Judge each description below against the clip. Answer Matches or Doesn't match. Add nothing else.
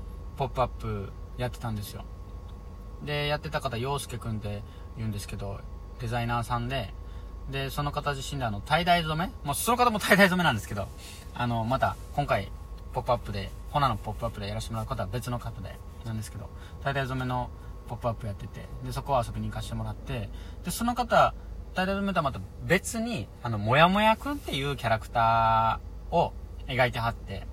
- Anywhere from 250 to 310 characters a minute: Doesn't match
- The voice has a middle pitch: Doesn't match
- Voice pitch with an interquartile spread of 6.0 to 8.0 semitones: Doesn't match